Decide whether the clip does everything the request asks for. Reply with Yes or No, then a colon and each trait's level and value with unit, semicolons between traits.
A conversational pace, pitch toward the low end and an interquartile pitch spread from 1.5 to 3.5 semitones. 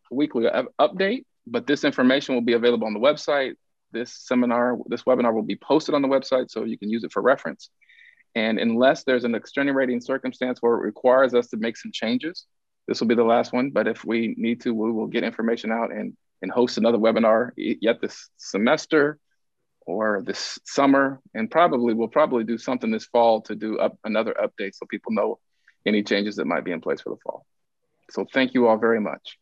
No: fast, 210 wpm; low, 120 Hz; average, 2.9 semitones